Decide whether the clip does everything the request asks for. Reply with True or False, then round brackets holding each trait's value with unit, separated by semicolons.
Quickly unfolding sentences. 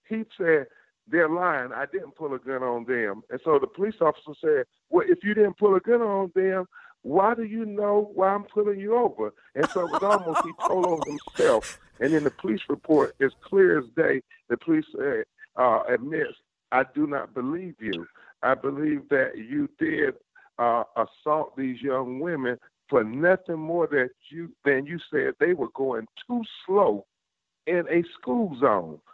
False (185 wpm)